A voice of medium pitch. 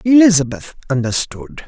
Yes: medium, 160 Hz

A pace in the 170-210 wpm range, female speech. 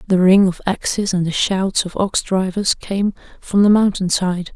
Yes: average, 200 wpm; female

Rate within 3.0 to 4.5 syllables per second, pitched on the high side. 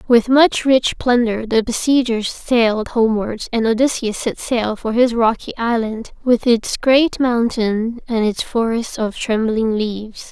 Yes: 4.1 syllables/s; high, 230 Hz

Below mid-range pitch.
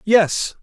No: high, 200 Hz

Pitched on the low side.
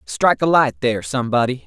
Yes: low, 125 Hz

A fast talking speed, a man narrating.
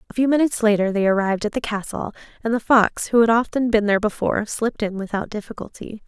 No: fast, 215 wpm; female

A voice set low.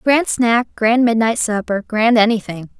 No: high, 225 Hz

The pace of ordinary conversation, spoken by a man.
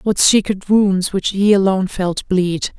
No: average, 170 wpm; female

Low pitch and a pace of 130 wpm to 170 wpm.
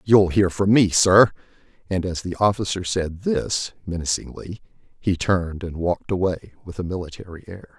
Yes: very low, 90 Hz; average, 160 wpm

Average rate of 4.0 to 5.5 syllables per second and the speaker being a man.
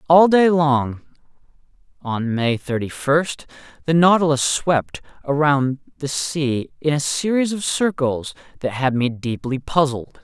No: 3.8 syllables/s; male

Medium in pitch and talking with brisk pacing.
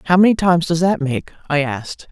Yes: medium, 165 Hz; fast, 225 wpm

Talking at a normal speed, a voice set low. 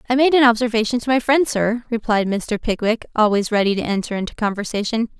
No: average, 195 wpm; high, 225 Hz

